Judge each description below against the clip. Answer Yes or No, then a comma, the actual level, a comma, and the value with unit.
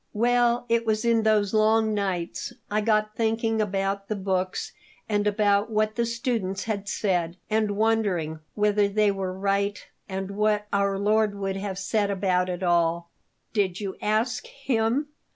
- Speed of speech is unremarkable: Yes, average, 155 wpm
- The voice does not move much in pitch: Yes, narrow, 2.2 semitones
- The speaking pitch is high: Yes, high, 205 Hz